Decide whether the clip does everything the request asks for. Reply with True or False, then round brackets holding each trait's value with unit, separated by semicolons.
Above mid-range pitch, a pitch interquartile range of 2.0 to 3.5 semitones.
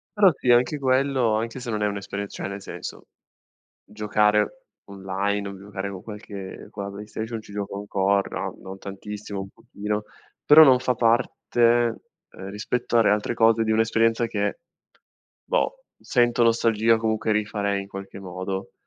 False (105 Hz; 2.5 semitones)